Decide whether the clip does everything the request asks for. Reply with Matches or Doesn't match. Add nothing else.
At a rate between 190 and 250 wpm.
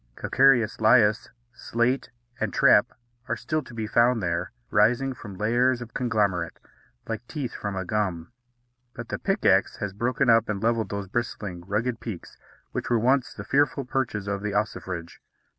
Doesn't match